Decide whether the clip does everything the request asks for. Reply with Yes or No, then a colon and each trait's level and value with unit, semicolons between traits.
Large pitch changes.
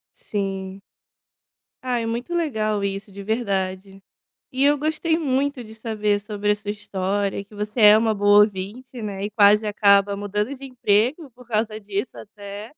No: average, 3.0 semitones